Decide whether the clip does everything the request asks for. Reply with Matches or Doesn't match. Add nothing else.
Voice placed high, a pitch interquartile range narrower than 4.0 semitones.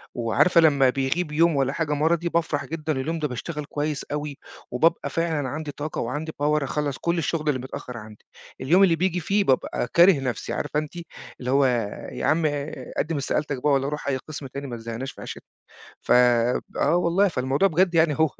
Doesn't match